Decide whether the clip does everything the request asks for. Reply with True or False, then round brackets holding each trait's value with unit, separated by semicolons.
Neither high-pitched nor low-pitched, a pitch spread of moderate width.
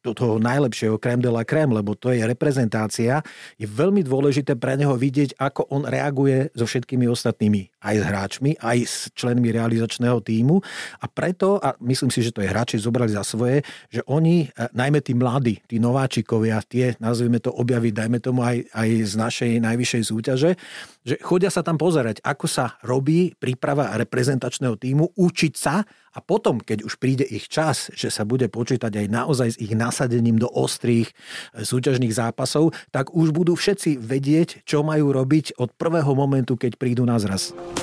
False (125 Hz; 3.6 semitones)